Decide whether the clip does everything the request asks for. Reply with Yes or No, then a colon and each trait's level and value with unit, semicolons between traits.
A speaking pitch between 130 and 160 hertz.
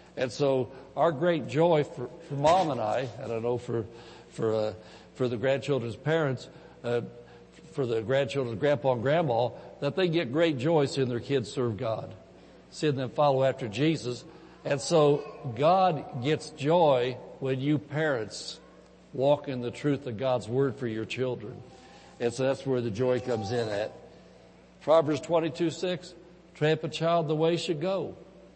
Yes: low, 135 Hz